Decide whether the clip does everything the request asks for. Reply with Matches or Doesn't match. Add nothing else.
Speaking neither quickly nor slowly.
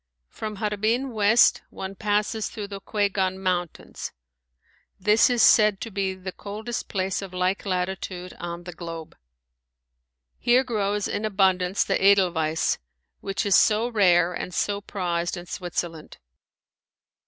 Doesn't match